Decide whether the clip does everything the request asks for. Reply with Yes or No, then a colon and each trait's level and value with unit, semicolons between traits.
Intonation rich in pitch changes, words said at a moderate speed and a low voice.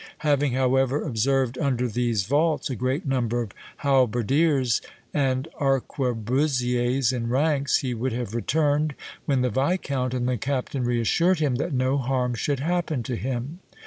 No: narrow, 2.6 semitones; average, 145 wpm; low, 130 Hz